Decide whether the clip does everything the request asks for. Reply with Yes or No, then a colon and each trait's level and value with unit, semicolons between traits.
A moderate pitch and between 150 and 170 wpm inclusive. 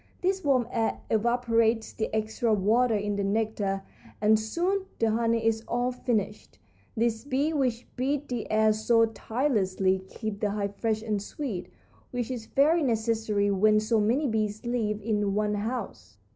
No: high, 220 Hz; average, 160 wpm